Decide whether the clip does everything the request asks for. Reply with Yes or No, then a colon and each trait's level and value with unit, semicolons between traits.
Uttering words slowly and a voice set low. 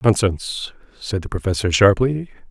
Yes: slow, 120 wpm; low, 105 Hz